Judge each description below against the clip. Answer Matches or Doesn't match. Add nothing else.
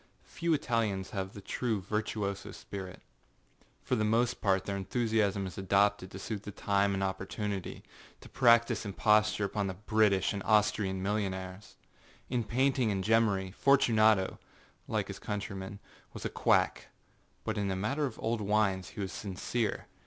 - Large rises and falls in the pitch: Doesn't match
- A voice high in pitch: Doesn't match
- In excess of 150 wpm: Doesn't match